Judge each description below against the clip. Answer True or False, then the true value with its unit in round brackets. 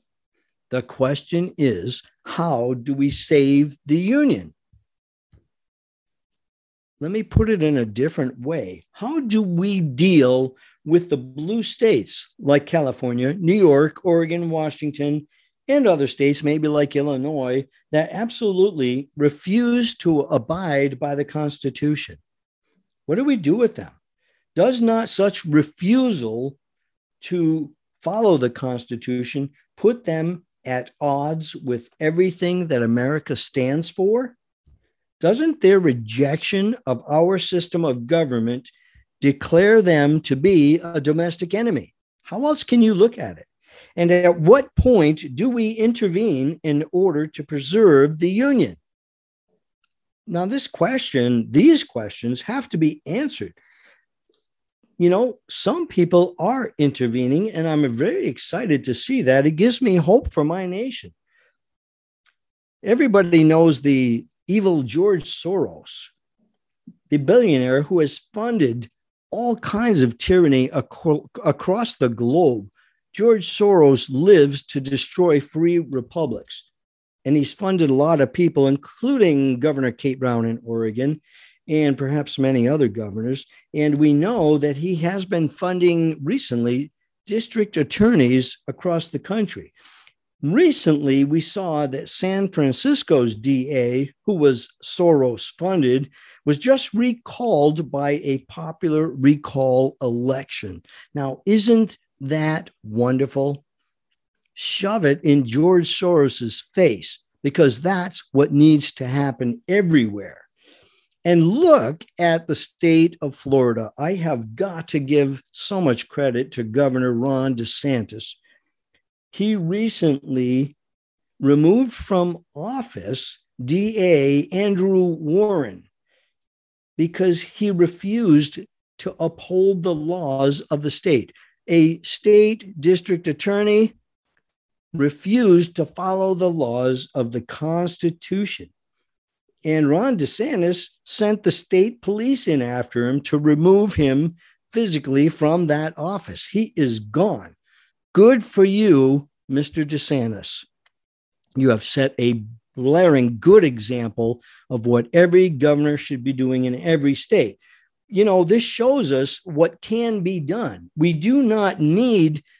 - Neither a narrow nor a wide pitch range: False (5.7 semitones)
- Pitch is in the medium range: True (155 Hz)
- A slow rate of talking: True (120 wpm)